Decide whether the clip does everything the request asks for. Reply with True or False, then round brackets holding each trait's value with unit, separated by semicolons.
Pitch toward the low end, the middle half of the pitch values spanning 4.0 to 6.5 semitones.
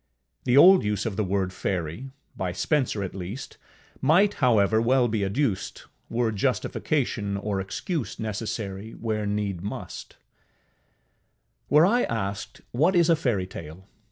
True (110 Hz; 5.2 semitones)